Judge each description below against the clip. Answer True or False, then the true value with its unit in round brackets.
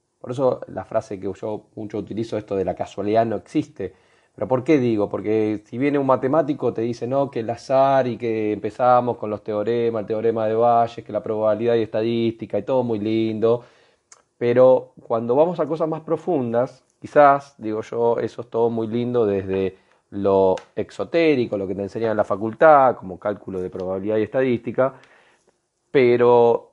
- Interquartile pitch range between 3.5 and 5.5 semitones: False (2.6 semitones)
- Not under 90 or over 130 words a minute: False (180 wpm)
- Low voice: True (115 Hz)